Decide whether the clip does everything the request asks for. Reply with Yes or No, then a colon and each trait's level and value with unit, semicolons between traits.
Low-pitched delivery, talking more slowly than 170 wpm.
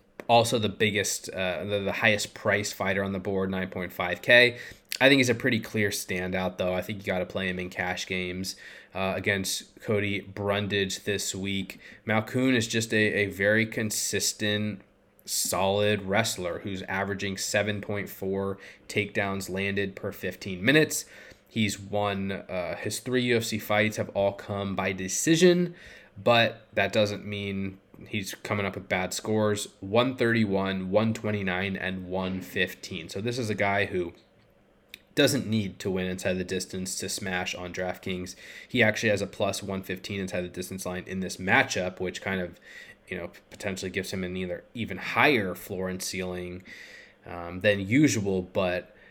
Yes: low, 100 Hz; average, 160 wpm